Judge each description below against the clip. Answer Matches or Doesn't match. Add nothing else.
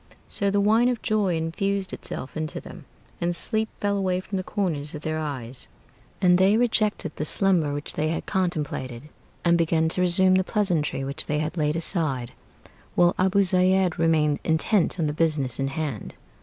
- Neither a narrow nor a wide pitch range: Matches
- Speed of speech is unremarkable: Matches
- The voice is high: Doesn't match